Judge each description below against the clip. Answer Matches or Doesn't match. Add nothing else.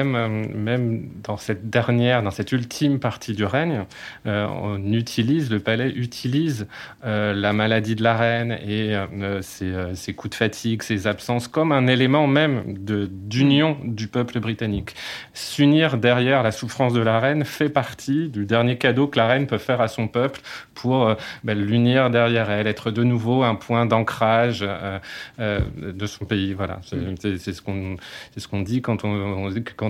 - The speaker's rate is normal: Matches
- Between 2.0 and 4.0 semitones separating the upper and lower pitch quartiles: Matches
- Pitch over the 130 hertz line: Doesn't match